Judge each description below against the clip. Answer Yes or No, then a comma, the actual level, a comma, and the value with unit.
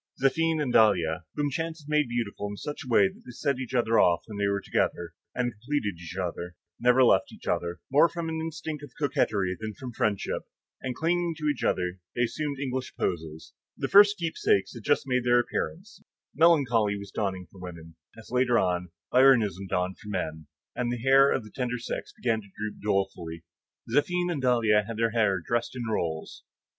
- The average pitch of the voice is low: Yes, low, 120 Hz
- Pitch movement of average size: No, wide, 6.0 semitones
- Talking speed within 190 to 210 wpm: Yes, average, 195 wpm